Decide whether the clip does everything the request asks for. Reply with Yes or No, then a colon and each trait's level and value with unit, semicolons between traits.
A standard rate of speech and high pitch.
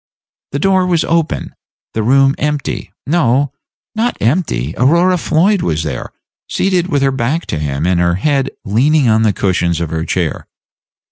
No: average, 160 wpm; low, 135 Hz